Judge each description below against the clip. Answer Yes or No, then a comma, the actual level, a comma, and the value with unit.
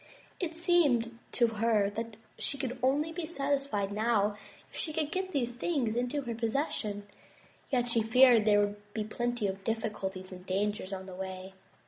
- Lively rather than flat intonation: No, average, 5.0 semitones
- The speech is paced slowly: No, average, 170 wpm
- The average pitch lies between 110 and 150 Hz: No, high, 230 Hz